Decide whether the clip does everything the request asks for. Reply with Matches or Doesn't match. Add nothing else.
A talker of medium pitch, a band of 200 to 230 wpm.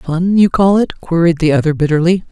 Matches